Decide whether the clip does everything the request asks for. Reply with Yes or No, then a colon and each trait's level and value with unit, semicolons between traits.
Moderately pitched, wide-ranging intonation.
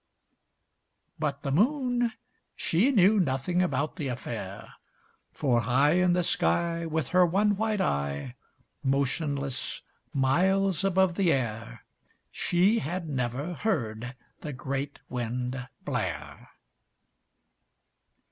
Yes: medium, 155 Hz; wide, 6.0 semitones